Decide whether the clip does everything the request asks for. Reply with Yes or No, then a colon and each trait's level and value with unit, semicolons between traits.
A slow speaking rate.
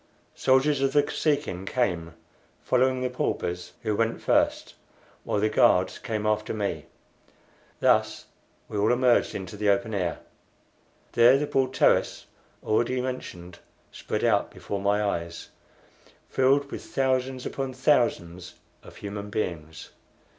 Yes: slow, 130 wpm